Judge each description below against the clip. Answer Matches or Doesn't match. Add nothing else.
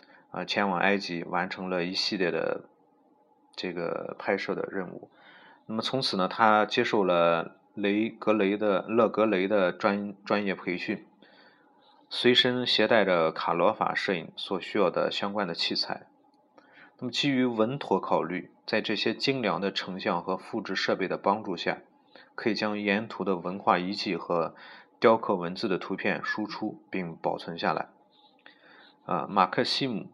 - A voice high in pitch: Doesn't match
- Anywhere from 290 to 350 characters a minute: Doesn't match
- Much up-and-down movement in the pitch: Doesn't match